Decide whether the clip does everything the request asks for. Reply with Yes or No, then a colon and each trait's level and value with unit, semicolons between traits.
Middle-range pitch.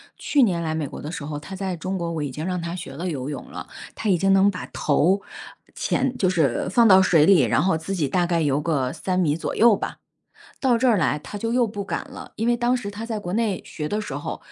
Yes: medium, 180 Hz